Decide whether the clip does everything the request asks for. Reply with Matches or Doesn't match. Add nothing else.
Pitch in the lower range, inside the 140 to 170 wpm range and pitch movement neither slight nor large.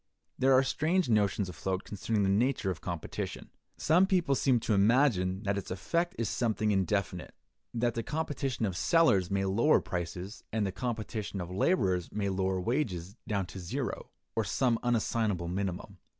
Matches